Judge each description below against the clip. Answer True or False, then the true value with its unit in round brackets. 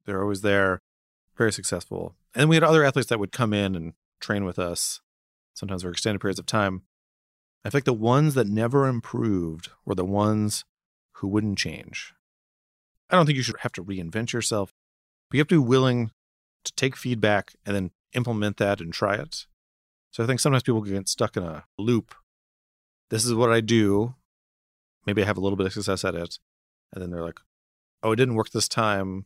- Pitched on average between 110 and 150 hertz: False (100 Hz)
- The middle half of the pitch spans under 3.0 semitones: False (4.8 semitones)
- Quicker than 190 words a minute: True (200 wpm)